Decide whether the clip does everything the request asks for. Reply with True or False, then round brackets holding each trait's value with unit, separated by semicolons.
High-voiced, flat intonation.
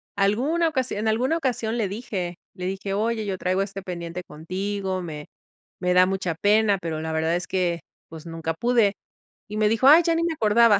False (195 Hz; 4.0 semitones)